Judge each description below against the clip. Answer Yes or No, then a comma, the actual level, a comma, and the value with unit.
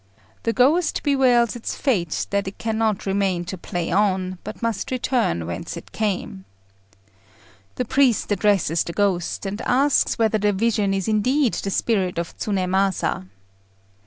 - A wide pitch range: No, average, 3.9 semitones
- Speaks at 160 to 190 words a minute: No, average, 145 wpm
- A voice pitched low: No, high, 205 Hz